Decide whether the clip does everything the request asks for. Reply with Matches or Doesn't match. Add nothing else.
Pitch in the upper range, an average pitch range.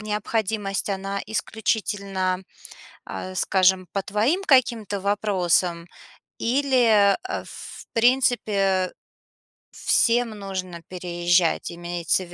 Matches